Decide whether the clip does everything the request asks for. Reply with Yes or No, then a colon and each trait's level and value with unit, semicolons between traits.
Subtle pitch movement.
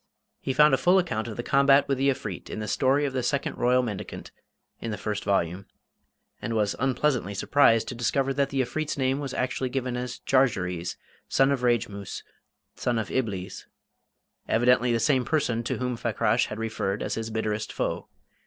No: average, 3.7 semitones